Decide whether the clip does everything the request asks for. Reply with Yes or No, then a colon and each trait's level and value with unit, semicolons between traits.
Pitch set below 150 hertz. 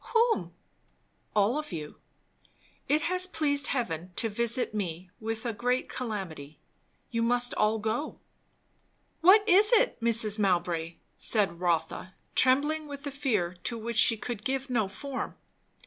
No: high, 230 Hz